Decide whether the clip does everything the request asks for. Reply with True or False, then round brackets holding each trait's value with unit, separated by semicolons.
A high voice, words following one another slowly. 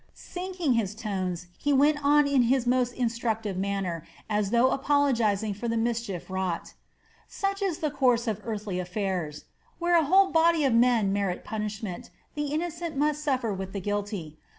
False (230 Hz; 165 wpm)